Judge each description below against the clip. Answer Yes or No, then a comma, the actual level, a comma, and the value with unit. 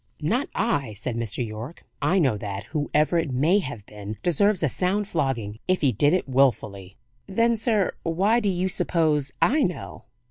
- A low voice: No, medium, 150 Hz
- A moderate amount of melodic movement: No, wide, 8.3 semitones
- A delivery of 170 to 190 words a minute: Yes, average, 175 wpm